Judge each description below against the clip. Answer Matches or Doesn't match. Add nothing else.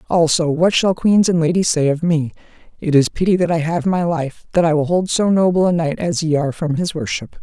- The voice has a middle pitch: Matches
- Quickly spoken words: Matches